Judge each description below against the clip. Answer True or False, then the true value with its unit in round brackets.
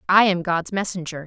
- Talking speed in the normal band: True (190 wpm)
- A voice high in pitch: False (180 Hz)